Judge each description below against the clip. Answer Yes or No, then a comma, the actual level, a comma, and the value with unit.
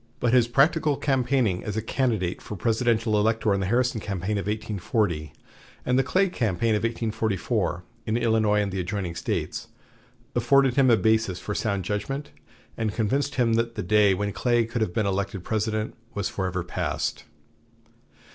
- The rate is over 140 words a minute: Yes, average, 165 wpm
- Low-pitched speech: Yes, low, 110 Hz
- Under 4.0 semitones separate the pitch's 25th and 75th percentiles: Yes, average, 3.1 semitones